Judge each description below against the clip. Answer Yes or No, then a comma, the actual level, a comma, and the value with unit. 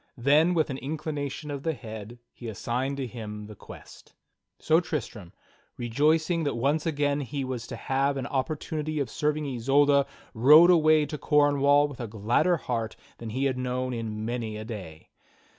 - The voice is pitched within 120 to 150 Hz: Yes, low, 135 Hz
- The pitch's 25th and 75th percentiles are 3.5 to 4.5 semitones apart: Yes, average, 4.2 semitones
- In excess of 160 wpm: Yes, average, 170 wpm